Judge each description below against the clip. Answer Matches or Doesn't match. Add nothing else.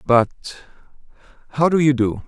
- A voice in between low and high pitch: Doesn't match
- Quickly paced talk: Doesn't match